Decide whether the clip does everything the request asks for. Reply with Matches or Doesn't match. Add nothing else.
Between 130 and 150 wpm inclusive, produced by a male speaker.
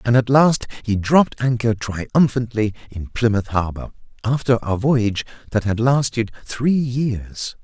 Matches